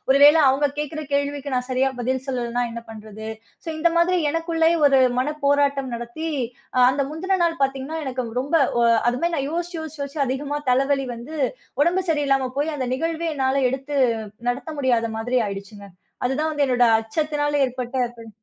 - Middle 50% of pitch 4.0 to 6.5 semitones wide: No, average, 3.6 semitones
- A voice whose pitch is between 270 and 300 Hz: Yes, very high, 275 Hz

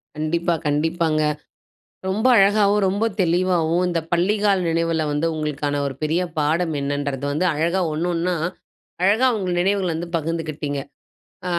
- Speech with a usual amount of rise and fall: Yes, average, 3.3 semitones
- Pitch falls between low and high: Yes, medium, 165 Hz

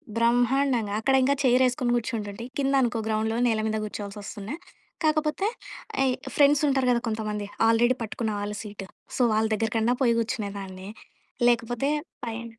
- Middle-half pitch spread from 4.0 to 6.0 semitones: No, average, 3.1 semitones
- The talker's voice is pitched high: Yes, high, 230 Hz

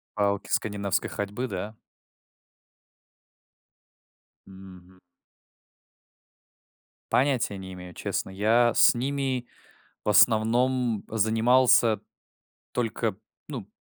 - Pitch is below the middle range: Yes, low, 110 Hz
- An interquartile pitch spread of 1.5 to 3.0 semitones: No, average, 3.6 semitones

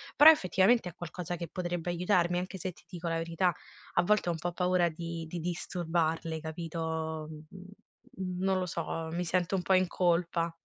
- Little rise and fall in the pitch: Yes, narrow, 1.7 semitones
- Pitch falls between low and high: Yes, medium, 175 Hz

